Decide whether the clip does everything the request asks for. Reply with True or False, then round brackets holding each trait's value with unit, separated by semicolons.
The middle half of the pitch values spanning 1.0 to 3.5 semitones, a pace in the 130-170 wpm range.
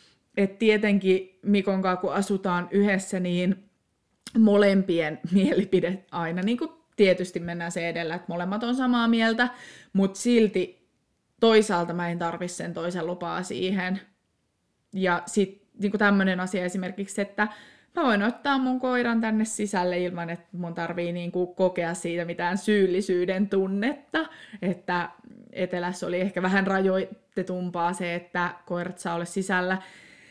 True (2.8 semitones; 135 wpm)